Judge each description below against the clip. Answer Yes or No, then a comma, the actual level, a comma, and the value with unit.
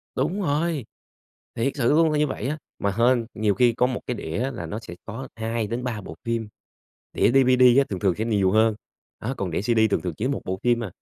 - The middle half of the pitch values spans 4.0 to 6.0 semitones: No, average, 3.6 semitones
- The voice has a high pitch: No, low, 115 Hz